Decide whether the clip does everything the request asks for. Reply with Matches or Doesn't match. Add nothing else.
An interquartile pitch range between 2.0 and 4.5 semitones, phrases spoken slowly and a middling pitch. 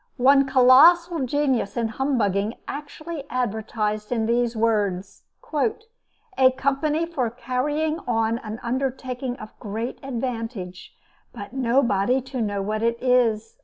Doesn't match